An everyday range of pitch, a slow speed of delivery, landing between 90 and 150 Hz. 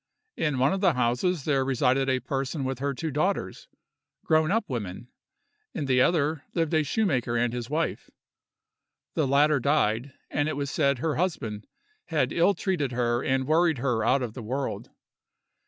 No: average, 3.9 semitones; average, 170 wpm; medium, 140 Hz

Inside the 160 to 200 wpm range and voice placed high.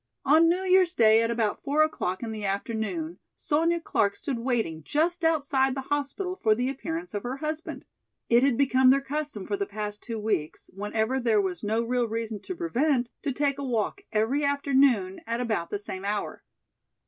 Yes: average, 190 wpm; very high, 250 Hz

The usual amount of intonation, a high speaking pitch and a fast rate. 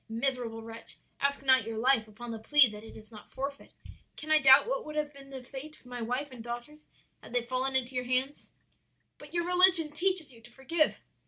Yes: average, 3.8 semitones; very high, 265 Hz; fast, 220 wpm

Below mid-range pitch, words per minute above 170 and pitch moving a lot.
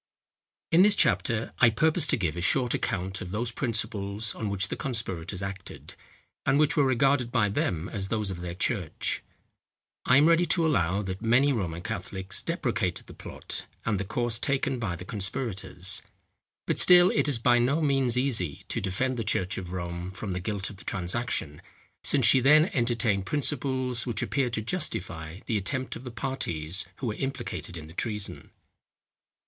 Yes: low, 110 Hz; average, 180 wpm; wide, 5.7 semitones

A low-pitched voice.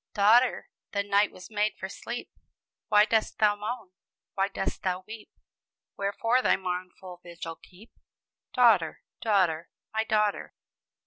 No: high, 205 Hz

